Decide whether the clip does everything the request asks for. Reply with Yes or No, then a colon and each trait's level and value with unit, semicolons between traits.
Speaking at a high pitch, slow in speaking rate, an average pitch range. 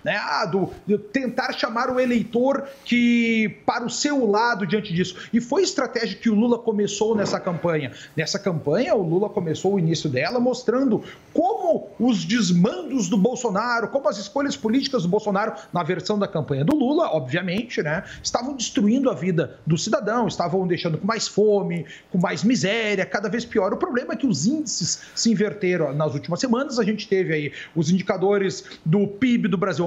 No: high, 210 Hz; fast, 185 wpm; average, 4.5 semitones